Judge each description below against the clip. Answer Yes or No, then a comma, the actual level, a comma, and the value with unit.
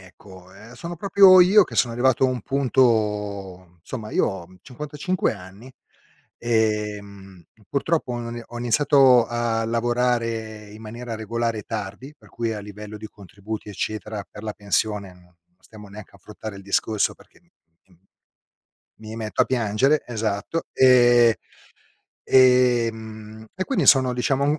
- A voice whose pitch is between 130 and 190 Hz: No, low, 110 Hz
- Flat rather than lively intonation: No, average, 3.2 semitones